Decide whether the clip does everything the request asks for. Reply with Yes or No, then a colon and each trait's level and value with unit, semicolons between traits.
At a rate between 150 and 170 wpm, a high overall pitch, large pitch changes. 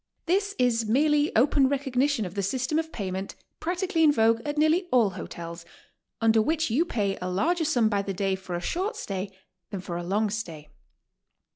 No: average, 185 wpm; high, 230 Hz; wide, 7.7 semitones